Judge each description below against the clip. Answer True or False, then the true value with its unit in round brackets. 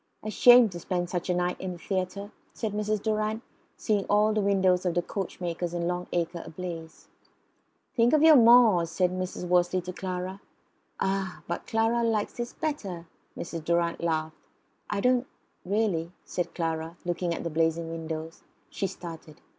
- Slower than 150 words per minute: False (170 wpm)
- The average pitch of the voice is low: False (180 Hz)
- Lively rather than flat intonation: False (3.6 semitones)